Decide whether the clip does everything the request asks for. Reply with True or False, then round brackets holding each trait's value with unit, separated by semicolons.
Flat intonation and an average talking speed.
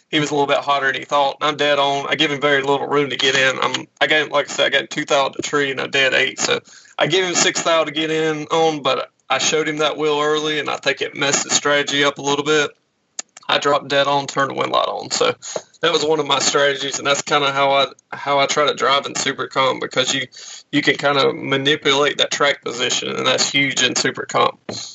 False (1.5 semitones; 260 wpm)